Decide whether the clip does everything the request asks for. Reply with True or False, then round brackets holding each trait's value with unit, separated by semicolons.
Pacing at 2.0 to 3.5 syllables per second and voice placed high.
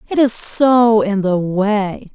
True (3.0 syllables/s; 215 Hz)